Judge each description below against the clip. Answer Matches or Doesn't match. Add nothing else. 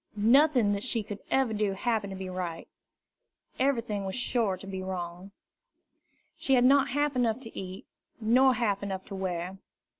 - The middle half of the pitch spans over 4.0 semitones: Matches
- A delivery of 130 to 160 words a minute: Doesn't match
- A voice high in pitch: Matches